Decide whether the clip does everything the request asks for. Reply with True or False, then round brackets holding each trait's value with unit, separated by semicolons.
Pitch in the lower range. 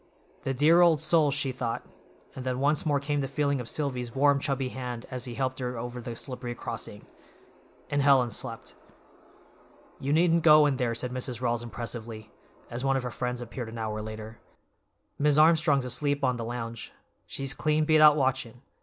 True (130 Hz)